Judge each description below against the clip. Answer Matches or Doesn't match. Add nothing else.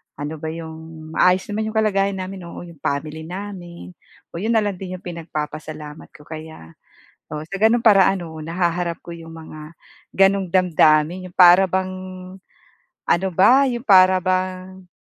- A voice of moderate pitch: Matches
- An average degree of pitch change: Matches